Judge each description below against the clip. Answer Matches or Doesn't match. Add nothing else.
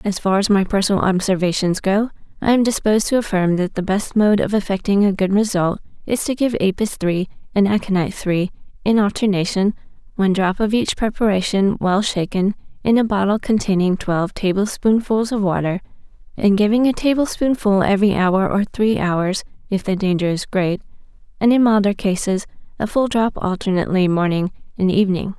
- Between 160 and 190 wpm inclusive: Matches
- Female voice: Matches